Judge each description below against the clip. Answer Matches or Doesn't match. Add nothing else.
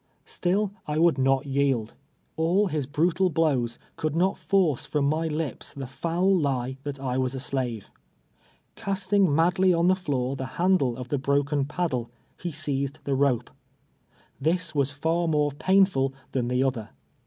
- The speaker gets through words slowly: Doesn't match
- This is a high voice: Doesn't match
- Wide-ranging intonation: Doesn't match